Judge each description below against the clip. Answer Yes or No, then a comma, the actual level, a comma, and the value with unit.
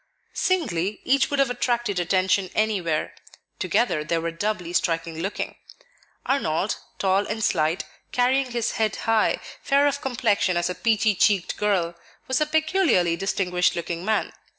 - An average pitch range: No, wide, 5.9 semitones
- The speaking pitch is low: No, high, 205 Hz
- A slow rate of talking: No, average, 145 wpm